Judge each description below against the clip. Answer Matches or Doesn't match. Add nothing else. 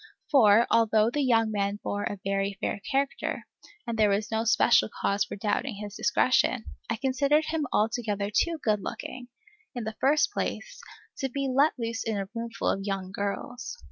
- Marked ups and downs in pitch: Doesn't match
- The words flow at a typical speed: Matches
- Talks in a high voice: Matches